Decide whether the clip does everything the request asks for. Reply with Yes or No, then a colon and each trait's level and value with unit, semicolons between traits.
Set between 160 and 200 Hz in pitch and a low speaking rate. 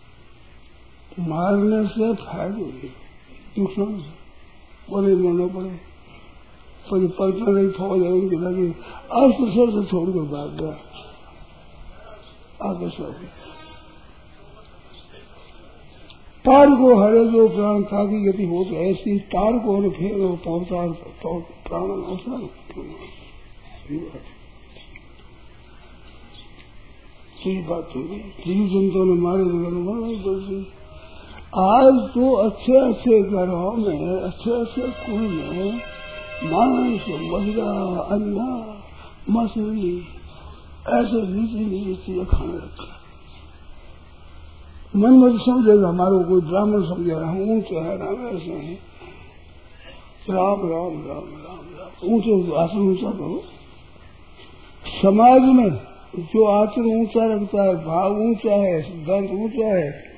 Yes: high, 190 Hz; slow, 75 wpm